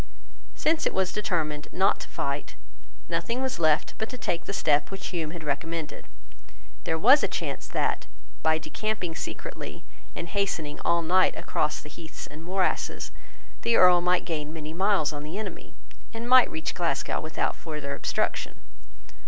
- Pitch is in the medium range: Yes, medium, 170 Hz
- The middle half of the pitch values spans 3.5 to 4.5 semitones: Yes, average, 3.8 semitones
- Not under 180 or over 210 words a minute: No, average, 160 wpm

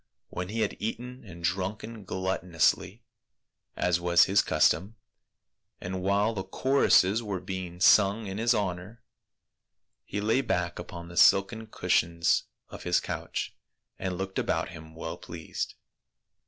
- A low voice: Yes, very low, 95 Hz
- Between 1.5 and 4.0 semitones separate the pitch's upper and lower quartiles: Yes, average, 3.4 semitones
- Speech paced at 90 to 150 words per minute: Yes, slow, 135 wpm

